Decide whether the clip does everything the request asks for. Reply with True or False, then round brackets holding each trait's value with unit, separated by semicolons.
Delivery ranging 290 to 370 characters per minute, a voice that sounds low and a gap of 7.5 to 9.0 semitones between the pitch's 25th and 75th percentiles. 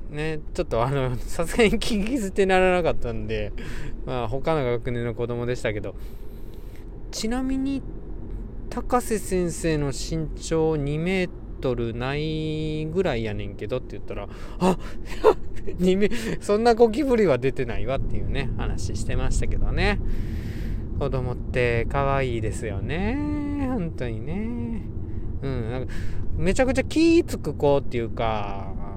False (275 characters per minute; 125 Hz; 7.9 semitones)